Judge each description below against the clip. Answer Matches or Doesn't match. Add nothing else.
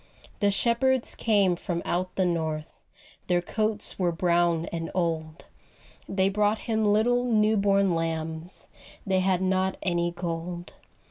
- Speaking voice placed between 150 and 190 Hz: Matches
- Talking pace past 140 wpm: Doesn't match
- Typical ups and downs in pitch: Matches